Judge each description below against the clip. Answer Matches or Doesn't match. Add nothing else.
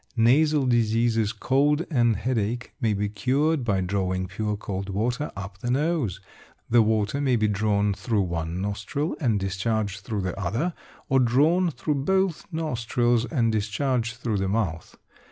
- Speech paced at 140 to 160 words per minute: Matches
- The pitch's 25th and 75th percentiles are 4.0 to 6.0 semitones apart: Matches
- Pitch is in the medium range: Doesn't match